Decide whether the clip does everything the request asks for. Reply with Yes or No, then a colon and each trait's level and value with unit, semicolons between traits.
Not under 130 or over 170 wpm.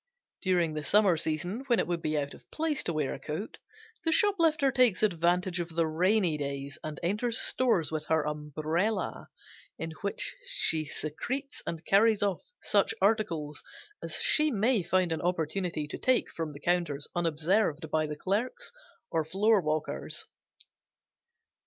Yes: average, 150 wpm